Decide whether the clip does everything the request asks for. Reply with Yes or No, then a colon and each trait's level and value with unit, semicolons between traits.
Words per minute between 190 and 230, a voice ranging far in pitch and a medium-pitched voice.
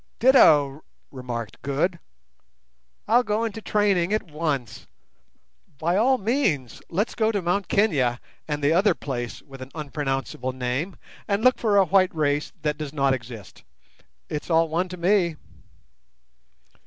No: average, 140 wpm; wide, 6.7 semitones; medium, 160 Hz